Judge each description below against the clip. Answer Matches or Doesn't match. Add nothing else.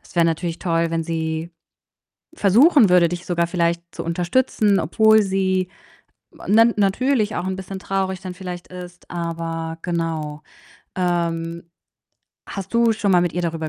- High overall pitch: Doesn't match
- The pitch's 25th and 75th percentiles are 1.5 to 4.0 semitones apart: Matches